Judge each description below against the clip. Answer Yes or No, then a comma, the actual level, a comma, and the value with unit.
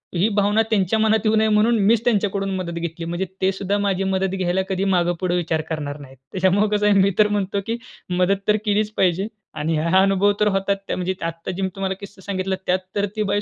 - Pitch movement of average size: No, narrow, 2.3 semitones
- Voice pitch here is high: Yes, high, 195 Hz